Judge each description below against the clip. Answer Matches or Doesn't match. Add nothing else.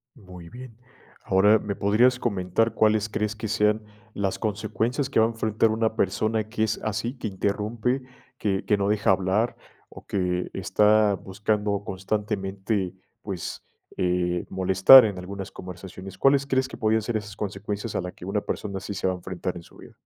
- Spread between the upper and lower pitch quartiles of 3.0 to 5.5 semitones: Doesn't match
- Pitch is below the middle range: Matches